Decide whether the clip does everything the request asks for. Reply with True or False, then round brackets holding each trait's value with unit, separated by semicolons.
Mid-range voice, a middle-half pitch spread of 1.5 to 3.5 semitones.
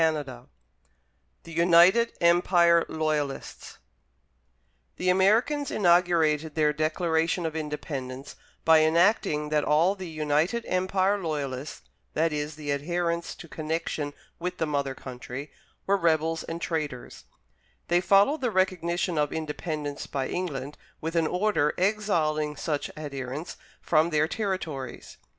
True (160 Hz; 3.0 semitones)